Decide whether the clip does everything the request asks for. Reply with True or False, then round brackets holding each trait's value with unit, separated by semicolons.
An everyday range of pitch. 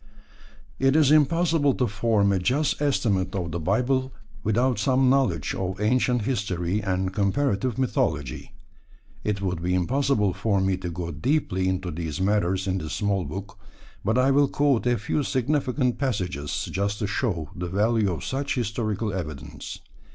False (5.8 semitones)